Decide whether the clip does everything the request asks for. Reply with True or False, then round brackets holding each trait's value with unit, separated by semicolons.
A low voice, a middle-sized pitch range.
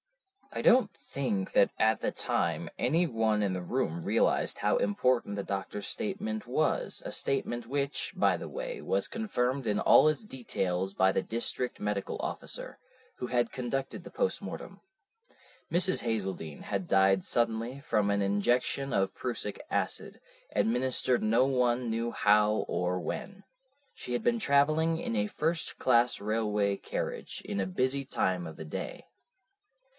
True (115 Hz; 5.0 semitones)